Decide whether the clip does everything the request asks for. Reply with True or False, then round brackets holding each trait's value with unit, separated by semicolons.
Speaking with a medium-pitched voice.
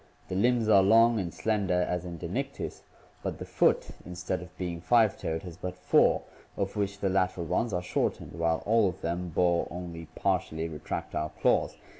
False (90 Hz)